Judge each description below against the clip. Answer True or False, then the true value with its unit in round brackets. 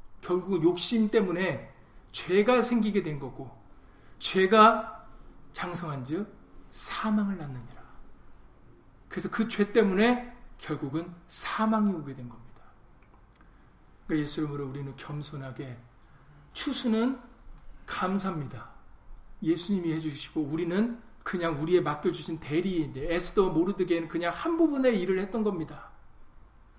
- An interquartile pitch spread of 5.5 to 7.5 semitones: True (6.4 semitones)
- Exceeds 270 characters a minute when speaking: False (255 characters per minute)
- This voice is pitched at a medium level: True (170 Hz)